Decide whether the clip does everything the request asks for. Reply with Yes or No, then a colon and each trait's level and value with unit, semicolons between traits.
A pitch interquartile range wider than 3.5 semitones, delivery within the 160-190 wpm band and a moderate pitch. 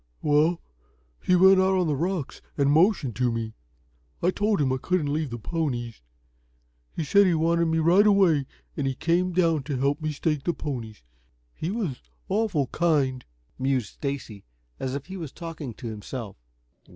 Yes: average, 4.9 semitones; average, 165 wpm; medium, 155 Hz